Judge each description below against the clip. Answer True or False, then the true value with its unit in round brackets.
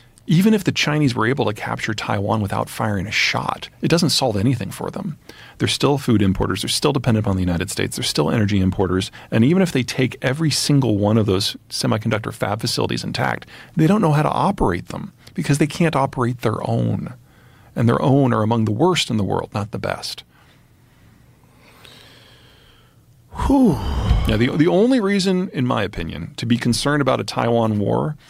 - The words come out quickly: False (190 wpm)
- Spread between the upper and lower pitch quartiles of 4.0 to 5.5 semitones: True (5.2 semitones)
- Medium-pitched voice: False (120 Hz)